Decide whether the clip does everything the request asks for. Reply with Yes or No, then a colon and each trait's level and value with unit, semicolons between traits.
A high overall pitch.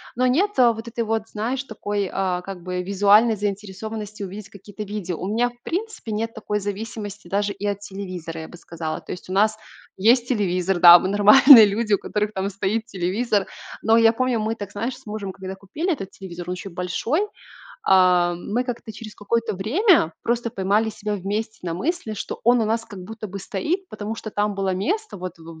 Yes: high, 205 Hz